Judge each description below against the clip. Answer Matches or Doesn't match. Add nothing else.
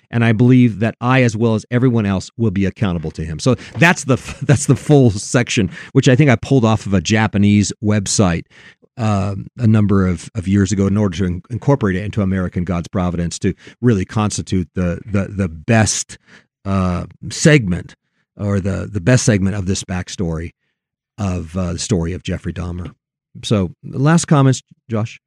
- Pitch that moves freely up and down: Doesn't match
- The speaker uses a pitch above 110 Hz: Doesn't match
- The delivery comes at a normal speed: Matches